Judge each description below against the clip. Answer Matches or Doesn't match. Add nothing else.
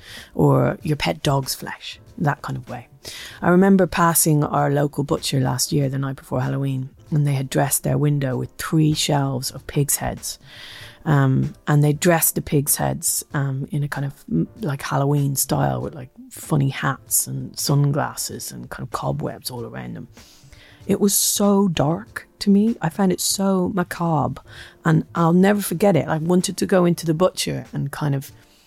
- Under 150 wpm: Doesn't match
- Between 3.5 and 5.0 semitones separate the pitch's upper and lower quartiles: Matches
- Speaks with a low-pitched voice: Doesn't match